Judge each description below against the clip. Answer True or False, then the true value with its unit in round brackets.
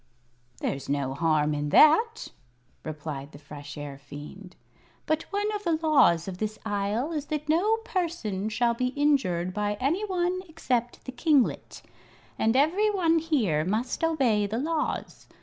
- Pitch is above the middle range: True (235 Hz)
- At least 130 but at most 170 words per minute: True (150 wpm)